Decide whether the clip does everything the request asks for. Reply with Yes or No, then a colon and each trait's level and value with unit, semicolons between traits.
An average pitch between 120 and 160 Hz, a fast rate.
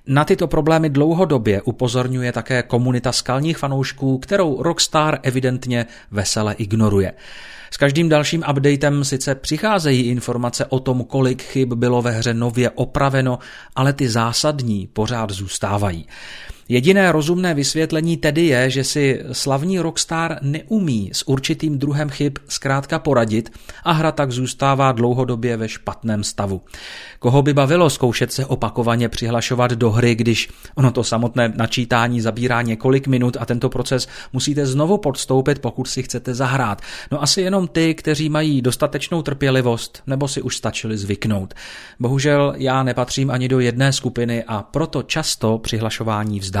No: low, 130 Hz; average, 145 wpm